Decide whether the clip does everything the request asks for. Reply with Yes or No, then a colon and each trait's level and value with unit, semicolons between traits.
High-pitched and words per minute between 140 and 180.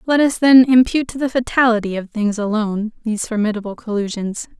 Yes: high, 225 Hz; average, 170 wpm